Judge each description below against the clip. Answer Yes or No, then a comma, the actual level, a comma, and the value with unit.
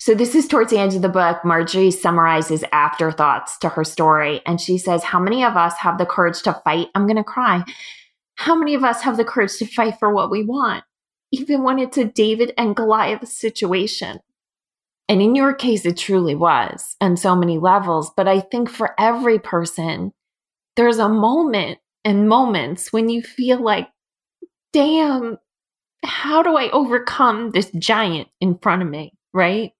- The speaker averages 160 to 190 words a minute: Yes, average, 180 wpm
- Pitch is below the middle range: No, high, 210 Hz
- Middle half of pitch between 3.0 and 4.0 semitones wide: No, wide, 5.4 semitones